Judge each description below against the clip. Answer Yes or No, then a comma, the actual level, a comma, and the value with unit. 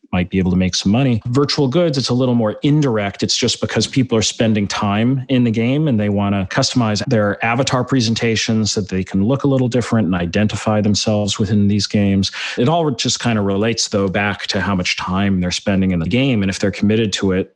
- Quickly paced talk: Yes, fast, 230 wpm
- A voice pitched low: Yes, low, 110 Hz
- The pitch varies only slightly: No, average, 3.8 semitones